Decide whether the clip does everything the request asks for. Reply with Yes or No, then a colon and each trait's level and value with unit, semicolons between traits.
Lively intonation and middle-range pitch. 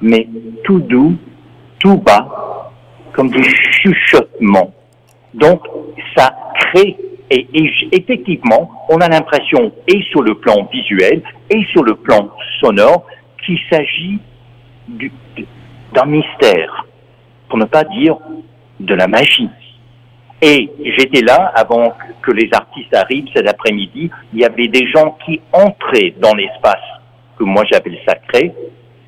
Yes: wide, 6.1 semitones; medium, 150 Hz